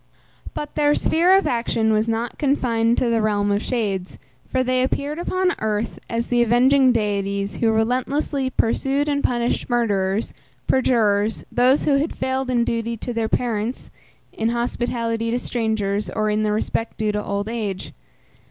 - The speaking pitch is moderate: No, high, 230 Hz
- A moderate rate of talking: Yes, average, 160 wpm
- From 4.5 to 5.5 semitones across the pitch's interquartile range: No, average, 3.1 semitones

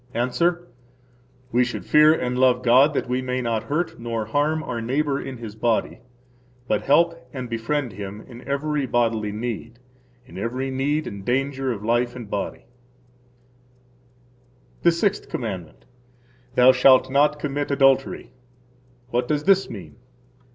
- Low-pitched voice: Yes, low, 125 Hz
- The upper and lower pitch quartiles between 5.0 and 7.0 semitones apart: No, average, 3.7 semitones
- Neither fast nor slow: Yes, average, 145 wpm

